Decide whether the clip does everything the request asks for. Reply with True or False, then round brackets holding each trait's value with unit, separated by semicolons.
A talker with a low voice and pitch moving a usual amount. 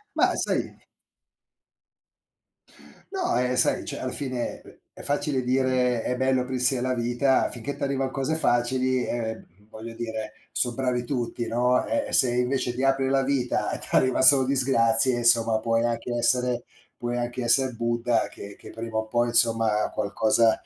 False (125 Hz; 1.9 semitones)